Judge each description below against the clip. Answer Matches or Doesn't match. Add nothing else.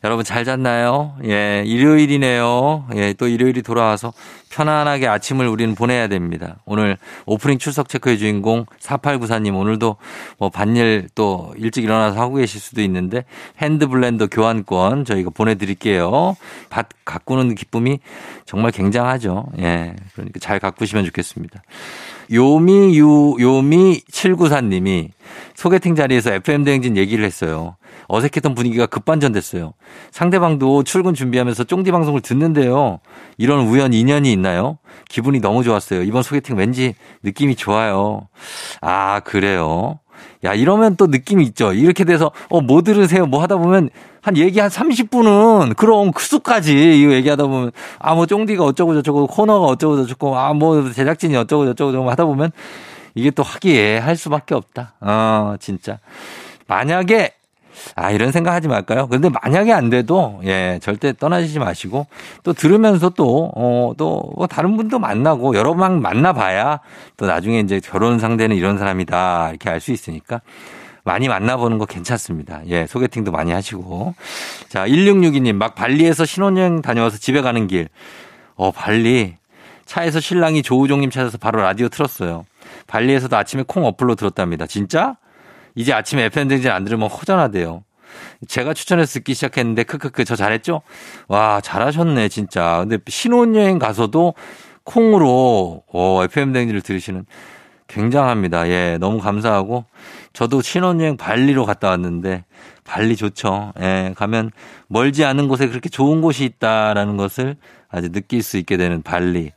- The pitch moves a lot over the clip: Matches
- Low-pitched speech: Matches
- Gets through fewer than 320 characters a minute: Doesn't match